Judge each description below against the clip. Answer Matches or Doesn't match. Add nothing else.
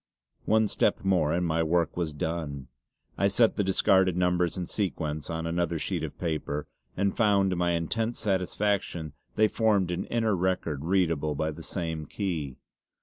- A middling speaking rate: Matches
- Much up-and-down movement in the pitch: Doesn't match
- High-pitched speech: Doesn't match